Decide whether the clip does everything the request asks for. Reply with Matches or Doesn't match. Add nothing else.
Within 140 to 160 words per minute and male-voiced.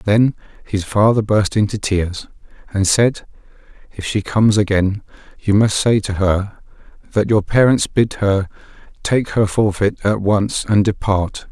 Matches